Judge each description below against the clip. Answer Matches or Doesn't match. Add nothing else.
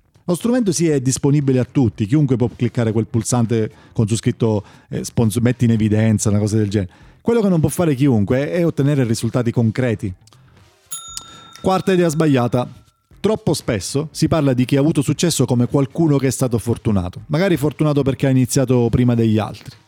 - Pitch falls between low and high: Doesn't match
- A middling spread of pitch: Matches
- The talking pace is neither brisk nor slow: Doesn't match